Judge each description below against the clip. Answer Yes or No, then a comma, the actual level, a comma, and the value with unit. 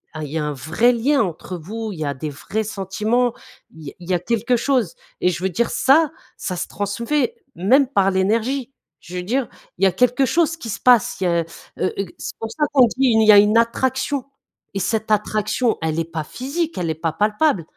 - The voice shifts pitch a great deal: Yes, wide, 5.8 semitones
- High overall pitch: Yes, high, 215 Hz